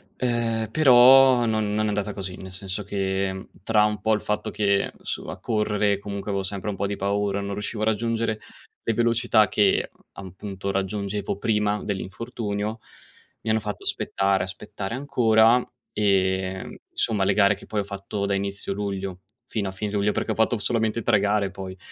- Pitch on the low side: Yes, low, 105 Hz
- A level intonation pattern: Yes, narrow, 2.0 semitones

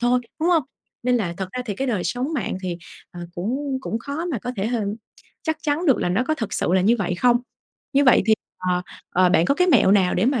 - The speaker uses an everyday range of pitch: No, wide, 6.8 semitones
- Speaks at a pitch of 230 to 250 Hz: Yes, high, 240 Hz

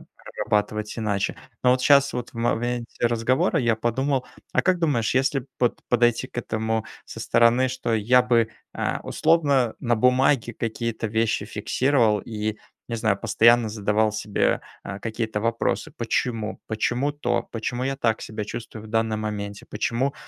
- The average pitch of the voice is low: Yes, low, 115 Hz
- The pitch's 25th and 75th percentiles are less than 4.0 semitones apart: Yes, narrow, 2.4 semitones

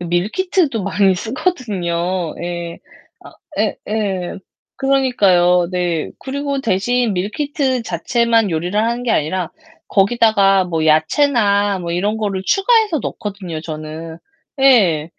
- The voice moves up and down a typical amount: No, wide, 5.7 semitones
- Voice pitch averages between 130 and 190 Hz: No, high, 200 Hz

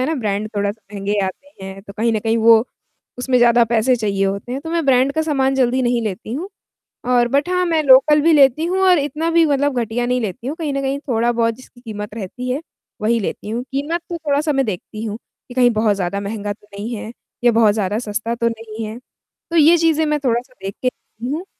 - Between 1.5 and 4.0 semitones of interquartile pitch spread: No, average, 4.6 semitones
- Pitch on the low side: No, high, 240 Hz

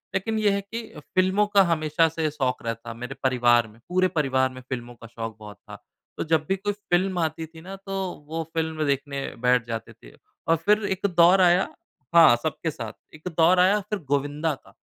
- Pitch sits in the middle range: Yes, medium, 160 Hz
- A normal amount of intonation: No, wide, 6.4 semitones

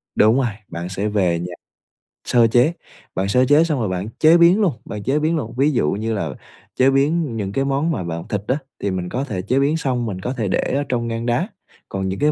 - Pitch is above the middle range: No, low, 120 Hz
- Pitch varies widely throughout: Yes, wide, 6.3 semitones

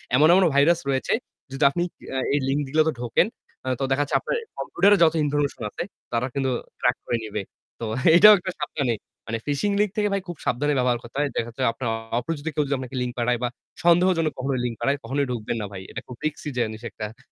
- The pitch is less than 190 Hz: Yes, medium, 140 Hz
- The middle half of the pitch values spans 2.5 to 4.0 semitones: No, average, 4.4 semitones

